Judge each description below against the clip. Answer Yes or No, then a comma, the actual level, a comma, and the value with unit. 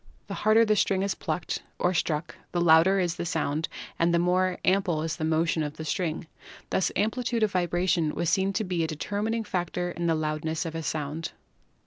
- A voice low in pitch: No, medium, 175 Hz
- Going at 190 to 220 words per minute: Yes, average, 200 wpm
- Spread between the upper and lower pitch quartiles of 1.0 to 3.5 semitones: Yes, average, 3.0 semitones